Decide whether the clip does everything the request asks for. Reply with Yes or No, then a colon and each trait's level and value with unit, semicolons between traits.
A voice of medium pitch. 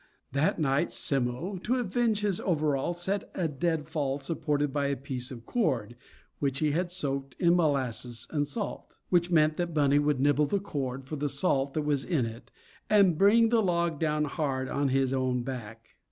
Yes: medium, 145 Hz